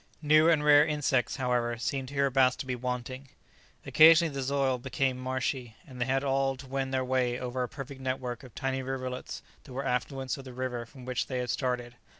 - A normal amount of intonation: No, narrow, 1.5 semitones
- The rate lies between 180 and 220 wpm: Yes, average, 200 wpm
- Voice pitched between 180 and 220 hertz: No, low, 130 Hz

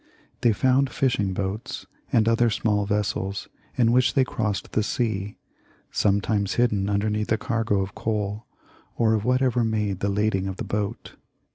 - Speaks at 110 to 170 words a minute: Yes, average, 155 wpm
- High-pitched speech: No, low, 105 Hz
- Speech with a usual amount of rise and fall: No, narrow, 2.3 semitones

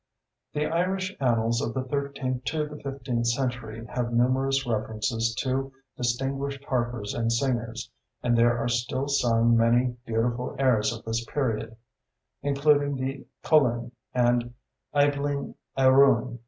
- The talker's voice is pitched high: No, low, 125 Hz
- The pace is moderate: No, slow, 130 wpm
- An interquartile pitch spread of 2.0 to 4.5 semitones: Yes, average, 2.8 semitones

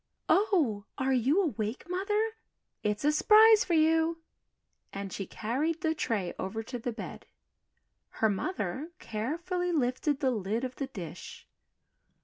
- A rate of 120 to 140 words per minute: Yes, slow, 135 wpm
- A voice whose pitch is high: Yes, very high, 265 Hz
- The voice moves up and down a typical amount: No, wide, 7.3 semitones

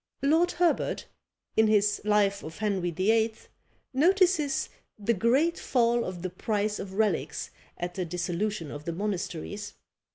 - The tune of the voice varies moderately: Yes, average, 4.3 semitones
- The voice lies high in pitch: Yes, high, 210 Hz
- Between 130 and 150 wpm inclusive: Yes, slow, 135 wpm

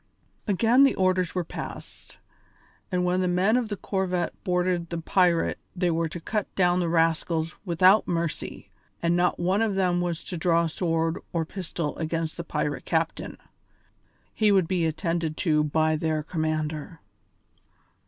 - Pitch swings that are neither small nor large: No, narrow, 2.2 semitones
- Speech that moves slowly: No, average, 155 wpm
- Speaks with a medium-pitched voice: Yes, medium, 175 Hz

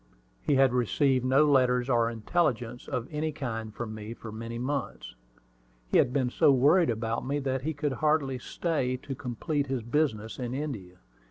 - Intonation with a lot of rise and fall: No, average, 3.5 semitones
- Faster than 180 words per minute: No, average, 175 wpm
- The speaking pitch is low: Yes, low, 130 Hz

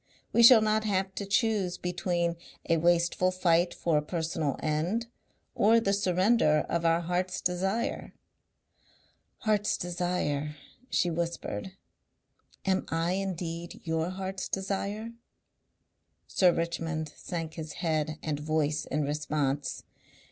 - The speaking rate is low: Yes, slow, 120 wpm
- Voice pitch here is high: No, medium, 175 Hz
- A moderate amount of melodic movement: Yes, average, 3.1 semitones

